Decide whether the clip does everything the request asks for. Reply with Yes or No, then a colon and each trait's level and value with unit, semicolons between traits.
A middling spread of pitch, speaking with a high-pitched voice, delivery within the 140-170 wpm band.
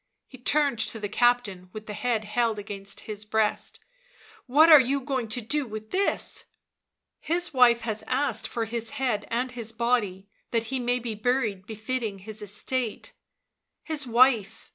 Yes: average, 3.1 semitones; high, 235 Hz; average, 165 wpm